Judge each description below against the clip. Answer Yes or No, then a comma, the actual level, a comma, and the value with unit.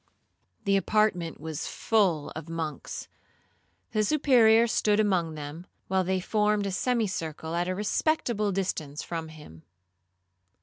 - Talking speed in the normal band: No, slow, 125 wpm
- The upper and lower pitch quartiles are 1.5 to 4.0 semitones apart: No, average, 4.8 semitones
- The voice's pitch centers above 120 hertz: Yes, high, 190 Hz